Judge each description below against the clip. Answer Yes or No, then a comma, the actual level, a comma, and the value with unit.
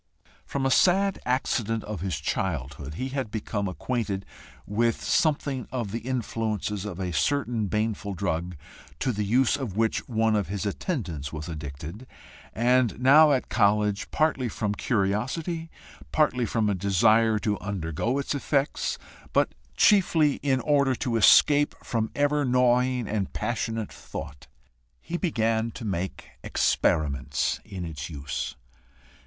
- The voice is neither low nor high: No, low, 110 Hz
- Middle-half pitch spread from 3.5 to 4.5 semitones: No, average, 5.1 semitones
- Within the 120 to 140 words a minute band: Yes, slow, 135 wpm